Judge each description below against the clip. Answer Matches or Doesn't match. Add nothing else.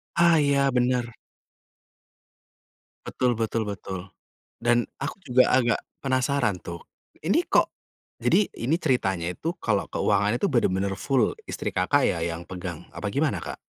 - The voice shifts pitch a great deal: Matches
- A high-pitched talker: Doesn't match